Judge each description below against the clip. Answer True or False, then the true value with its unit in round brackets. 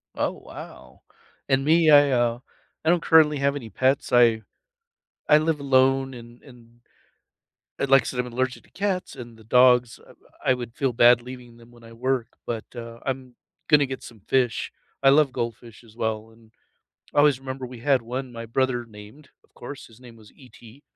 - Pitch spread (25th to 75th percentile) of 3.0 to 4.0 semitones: False (2.6 semitones)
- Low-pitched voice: True (125 Hz)